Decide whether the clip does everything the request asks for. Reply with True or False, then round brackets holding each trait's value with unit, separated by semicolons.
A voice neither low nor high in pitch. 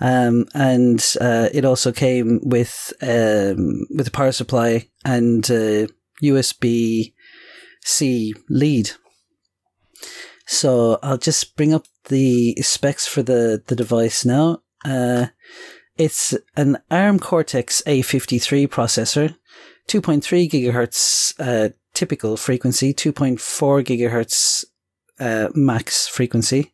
False (125 Hz)